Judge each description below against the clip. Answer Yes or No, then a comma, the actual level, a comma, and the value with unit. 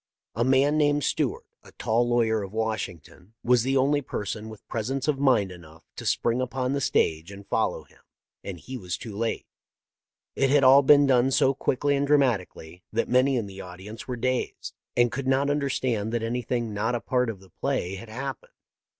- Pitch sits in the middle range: No, low, 120 Hz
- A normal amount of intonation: Yes, average, 4.2 semitones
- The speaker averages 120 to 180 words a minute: No, average, 200 wpm